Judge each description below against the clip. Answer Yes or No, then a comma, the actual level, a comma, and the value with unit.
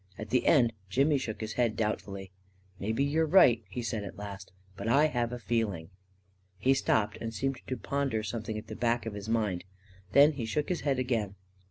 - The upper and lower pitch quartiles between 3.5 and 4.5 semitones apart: Yes, average, 3.9 semitones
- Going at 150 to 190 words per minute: No, fast, 205 wpm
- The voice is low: Yes, low, 115 Hz